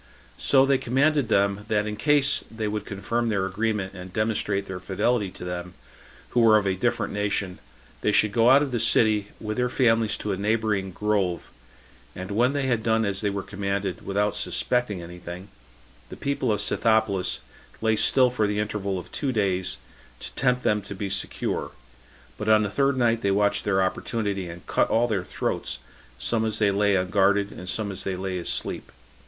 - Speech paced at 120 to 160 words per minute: No, average, 195 wpm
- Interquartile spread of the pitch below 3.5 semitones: Yes, average, 2.8 semitones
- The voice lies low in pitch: Yes, low, 105 Hz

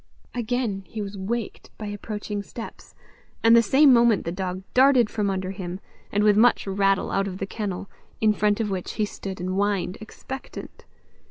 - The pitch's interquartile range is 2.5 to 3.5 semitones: Yes, average, 2.8 semitones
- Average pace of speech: Yes, average, 180 wpm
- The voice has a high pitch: Yes, high, 205 Hz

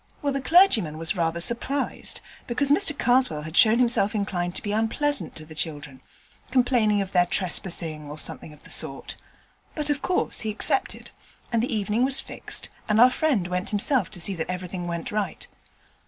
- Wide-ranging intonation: Yes, wide, 6.4 semitones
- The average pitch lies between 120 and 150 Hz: No, high, 210 Hz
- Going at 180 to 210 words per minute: Yes, average, 185 wpm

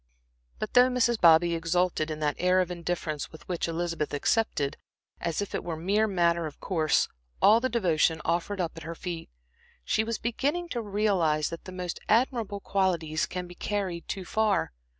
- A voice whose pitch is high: No, medium, 180 Hz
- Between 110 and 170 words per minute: No, average, 185 wpm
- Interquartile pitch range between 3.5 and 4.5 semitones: Yes, average, 4.1 semitones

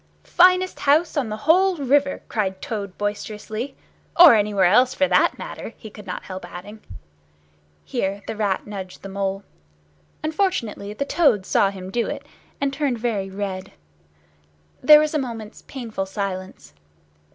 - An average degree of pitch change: No, wide, 6.2 semitones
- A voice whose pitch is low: No, high, 215 Hz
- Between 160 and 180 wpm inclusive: No, average, 150 wpm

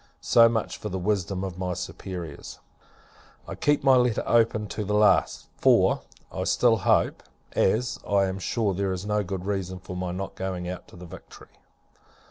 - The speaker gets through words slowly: No, average, 180 wpm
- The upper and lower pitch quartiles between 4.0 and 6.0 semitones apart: No, narrow, 2.6 semitones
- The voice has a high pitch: No, very low, 95 Hz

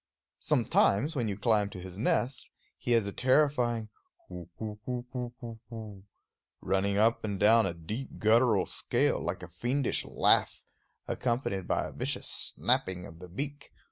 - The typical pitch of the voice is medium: No, low, 110 Hz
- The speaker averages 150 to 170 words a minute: Yes, average, 160 wpm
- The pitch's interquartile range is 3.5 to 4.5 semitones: Yes, average, 3.9 semitones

